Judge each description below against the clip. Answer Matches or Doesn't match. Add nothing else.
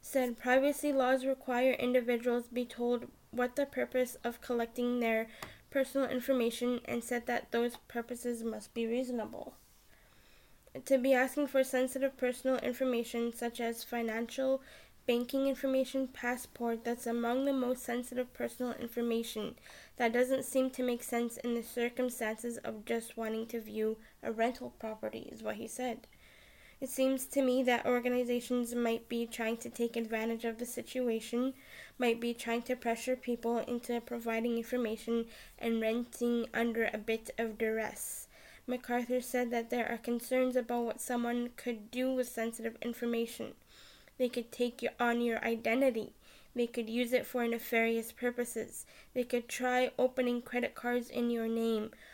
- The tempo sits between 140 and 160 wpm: Matches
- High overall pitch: Matches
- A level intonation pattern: Matches